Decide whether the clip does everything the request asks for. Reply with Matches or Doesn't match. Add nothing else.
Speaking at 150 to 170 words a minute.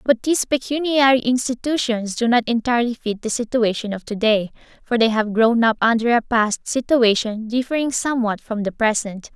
Matches